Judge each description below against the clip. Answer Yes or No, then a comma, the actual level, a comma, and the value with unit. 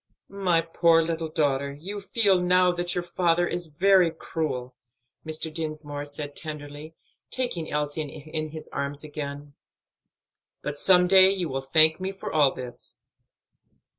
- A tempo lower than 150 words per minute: Yes, average, 140 wpm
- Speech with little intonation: No, average, 3.3 semitones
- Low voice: No, medium, 160 Hz